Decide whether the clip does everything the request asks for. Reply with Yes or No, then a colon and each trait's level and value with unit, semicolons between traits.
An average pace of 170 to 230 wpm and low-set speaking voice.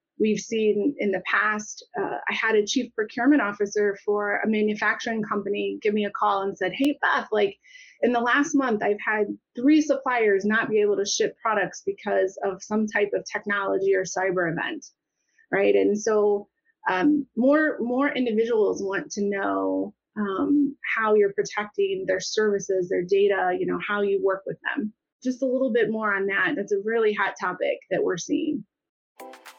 No: average, 180 wpm; high, 210 Hz